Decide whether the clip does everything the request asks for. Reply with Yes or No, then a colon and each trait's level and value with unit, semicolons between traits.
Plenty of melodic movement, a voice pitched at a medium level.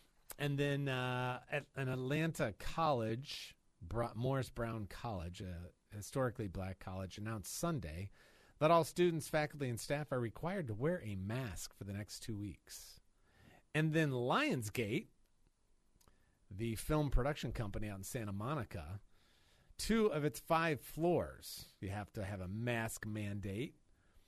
No: wide, 6.2 semitones; low, 115 Hz